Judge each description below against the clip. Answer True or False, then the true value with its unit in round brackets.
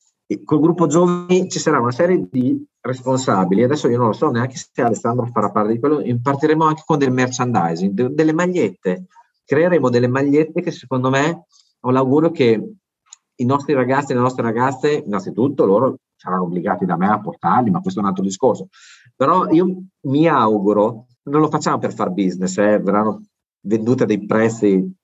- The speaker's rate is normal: False (180 wpm)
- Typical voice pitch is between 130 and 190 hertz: True (135 Hz)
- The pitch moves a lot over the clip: True (6.0 semitones)